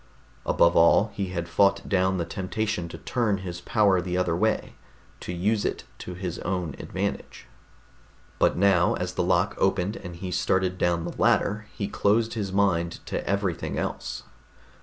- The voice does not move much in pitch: Yes, narrow, 2.3 semitones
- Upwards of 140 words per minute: Yes, average, 165 wpm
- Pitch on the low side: Yes, very low, 95 Hz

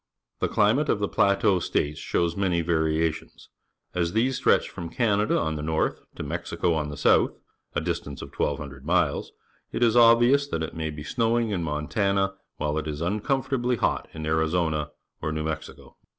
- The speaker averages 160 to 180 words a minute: No, average, 190 wpm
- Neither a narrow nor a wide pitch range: No, wide, 5.8 semitones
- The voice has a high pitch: No, very low, 85 Hz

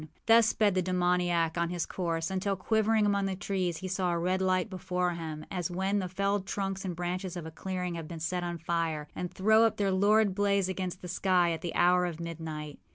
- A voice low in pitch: No, medium, 180 Hz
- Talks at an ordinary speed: No, fast, 220 wpm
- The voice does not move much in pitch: Yes, narrow, 2.2 semitones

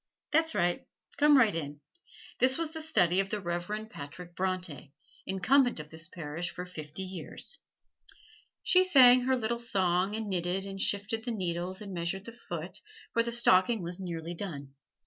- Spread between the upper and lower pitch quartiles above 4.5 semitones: Yes, average, 5.2 semitones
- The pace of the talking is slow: No, average, 165 wpm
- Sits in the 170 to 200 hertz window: Yes, high, 190 Hz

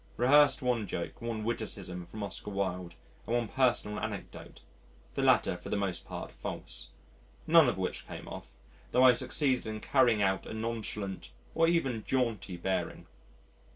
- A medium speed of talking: Yes, average, 155 wpm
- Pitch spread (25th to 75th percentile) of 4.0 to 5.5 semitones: Yes, average, 4.3 semitones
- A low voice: Yes, low, 110 Hz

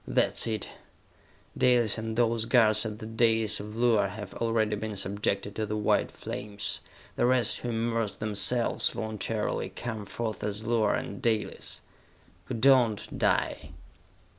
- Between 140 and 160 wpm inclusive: Yes, average, 145 wpm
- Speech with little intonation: Yes, narrow, 1.8 semitones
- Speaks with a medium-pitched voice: No, low, 110 Hz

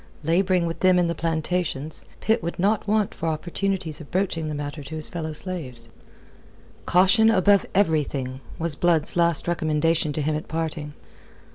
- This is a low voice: No, medium, 165 Hz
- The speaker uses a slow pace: No, average, 160 wpm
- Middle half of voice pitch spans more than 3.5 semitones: No, average, 3.0 semitones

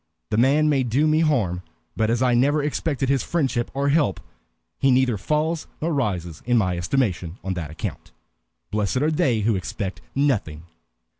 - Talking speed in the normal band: Yes, average, 170 wpm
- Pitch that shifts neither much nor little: No, wide, 6.5 semitones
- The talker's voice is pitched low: Yes, low, 125 Hz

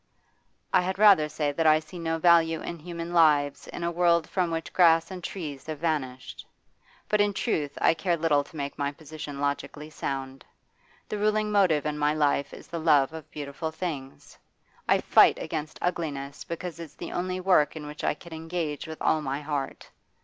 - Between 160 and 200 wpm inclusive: Yes, average, 190 wpm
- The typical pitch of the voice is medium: Yes, medium, 160 Hz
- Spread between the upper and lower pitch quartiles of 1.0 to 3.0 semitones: Yes, average, 2.7 semitones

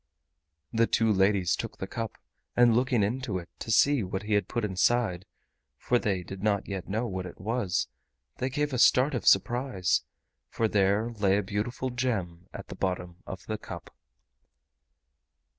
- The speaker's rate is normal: Yes, average, 160 wpm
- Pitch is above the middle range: No, low, 105 Hz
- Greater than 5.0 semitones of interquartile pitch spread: No, average, 4.2 semitones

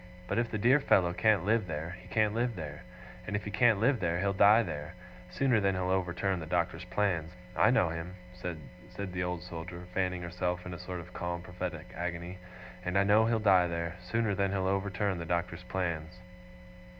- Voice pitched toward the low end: Yes, very low, 90 Hz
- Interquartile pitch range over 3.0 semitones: No, narrow, 2.5 semitones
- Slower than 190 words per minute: No, average, 200 wpm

